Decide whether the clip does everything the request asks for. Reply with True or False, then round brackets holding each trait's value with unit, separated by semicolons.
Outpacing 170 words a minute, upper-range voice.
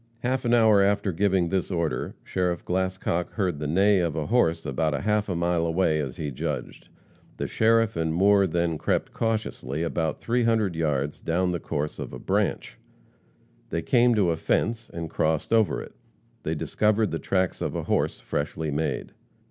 False (180 wpm; 90 Hz)